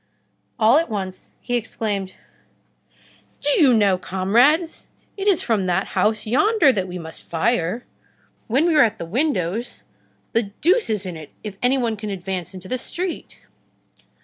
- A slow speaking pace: No, average, 160 wpm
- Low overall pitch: No, high, 220 Hz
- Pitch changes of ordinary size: No, wide, 6.1 semitones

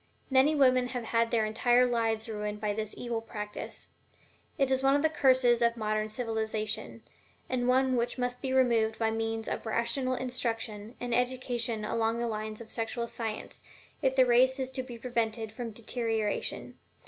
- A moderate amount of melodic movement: No, narrow, 2.3 semitones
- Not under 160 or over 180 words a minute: Yes, average, 170 wpm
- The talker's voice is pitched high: Yes, high, 235 Hz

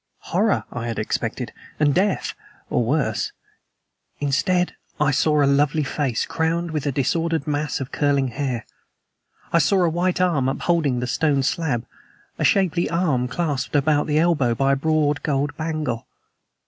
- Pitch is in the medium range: Yes, medium, 145 Hz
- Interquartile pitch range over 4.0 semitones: No, average, 3.3 semitones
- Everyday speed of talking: Yes, average, 155 wpm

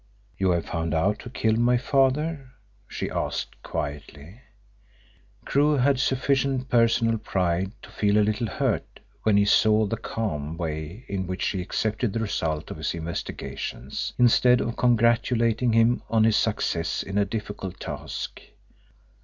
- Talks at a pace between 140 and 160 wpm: Yes, average, 145 wpm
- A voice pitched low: Yes, low, 110 Hz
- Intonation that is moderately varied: Yes, average, 4.9 semitones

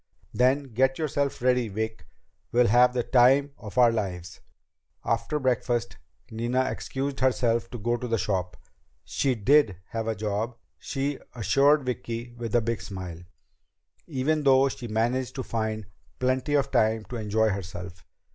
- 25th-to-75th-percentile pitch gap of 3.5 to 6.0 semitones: No, average, 3.1 semitones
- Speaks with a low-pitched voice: Yes, low, 120 Hz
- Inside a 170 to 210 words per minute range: No, average, 150 wpm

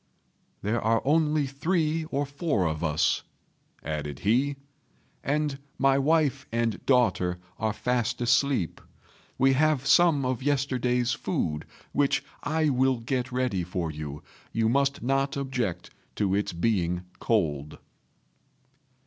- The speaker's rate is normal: No, slow, 125 wpm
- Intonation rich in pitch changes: Yes, wide, 5.9 semitones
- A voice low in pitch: Yes, low, 125 Hz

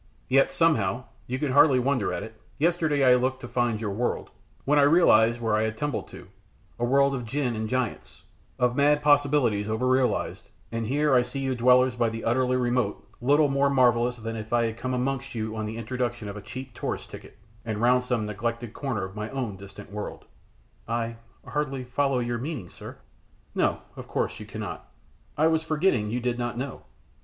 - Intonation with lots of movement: No, average, 3.2 semitones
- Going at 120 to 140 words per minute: No, average, 200 wpm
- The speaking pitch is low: Yes, low, 125 Hz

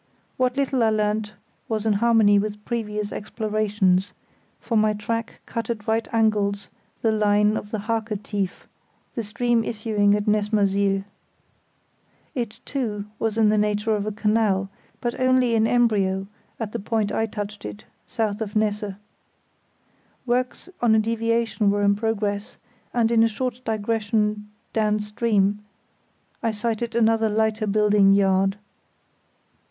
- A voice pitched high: Yes, high, 215 Hz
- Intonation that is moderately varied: No, narrow, 1.7 semitones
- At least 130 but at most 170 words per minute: Yes, average, 140 wpm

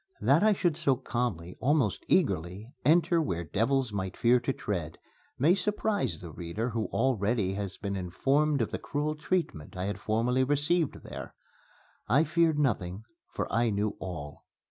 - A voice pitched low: Yes, low, 120 Hz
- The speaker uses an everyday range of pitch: No, wide, 7.4 semitones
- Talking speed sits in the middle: Yes, average, 160 wpm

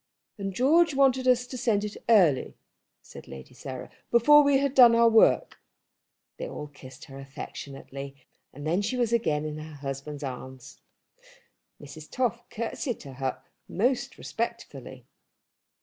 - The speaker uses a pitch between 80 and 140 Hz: No, high, 190 Hz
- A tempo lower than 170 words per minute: Yes, average, 145 wpm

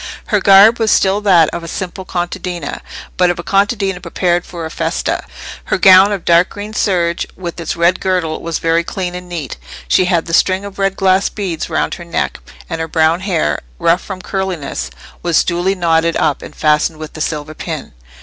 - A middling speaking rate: Yes, average, 195 wpm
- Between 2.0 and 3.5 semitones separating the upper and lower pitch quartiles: Yes, narrow, 2.5 semitones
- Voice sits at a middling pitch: Yes, medium, 175 Hz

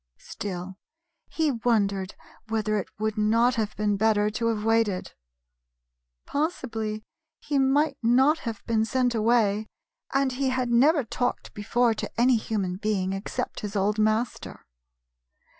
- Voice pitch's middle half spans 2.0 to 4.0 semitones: Yes, average, 2.9 semitones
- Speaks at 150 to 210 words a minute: No, slow, 135 wpm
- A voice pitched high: Yes, high, 225 Hz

